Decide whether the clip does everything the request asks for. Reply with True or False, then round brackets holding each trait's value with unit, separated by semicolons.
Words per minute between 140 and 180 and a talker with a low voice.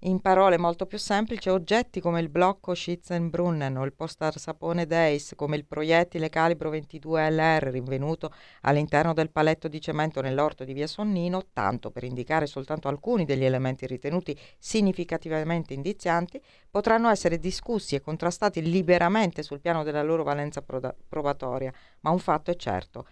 False (150 wpm; 160 Hz)